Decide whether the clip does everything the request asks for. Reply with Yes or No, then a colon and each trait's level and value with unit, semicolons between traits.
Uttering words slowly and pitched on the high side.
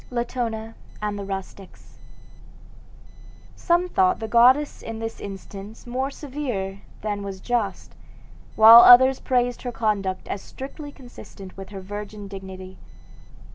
Yes: slow, 125 wpm; high, 220 Hz